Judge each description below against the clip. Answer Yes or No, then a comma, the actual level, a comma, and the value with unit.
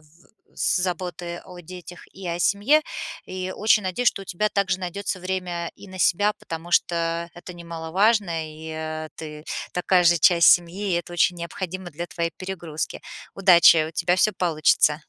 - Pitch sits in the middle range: Yes, medium, 175 Hz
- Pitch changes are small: Yes, narrow, 2.0 semitones